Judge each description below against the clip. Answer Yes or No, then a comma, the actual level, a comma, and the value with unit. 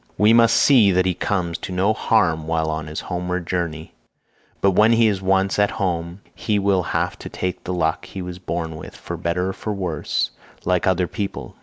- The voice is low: Yes, very low, 90 Hz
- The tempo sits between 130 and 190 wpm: No, average, 200 wpm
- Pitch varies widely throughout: No, average, 2.7 semitones